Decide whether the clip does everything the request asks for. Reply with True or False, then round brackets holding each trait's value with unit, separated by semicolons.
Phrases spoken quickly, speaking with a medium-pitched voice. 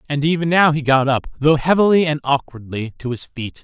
True (215 wpm; 145 Hz)